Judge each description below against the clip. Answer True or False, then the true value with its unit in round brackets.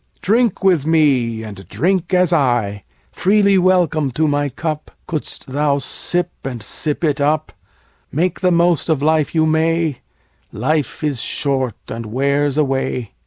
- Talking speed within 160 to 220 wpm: False (150 wpm)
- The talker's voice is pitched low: False (150 Hz)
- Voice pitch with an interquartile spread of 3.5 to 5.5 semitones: True (4.1 semitones)